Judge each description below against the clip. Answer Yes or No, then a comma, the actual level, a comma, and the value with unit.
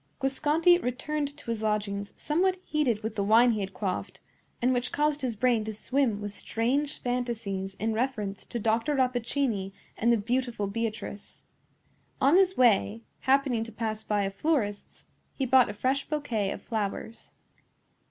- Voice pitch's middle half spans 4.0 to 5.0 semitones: Yes, average, 4.3 semitones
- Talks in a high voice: Yes, high, 235 Hz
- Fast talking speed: No, average, 160 wpm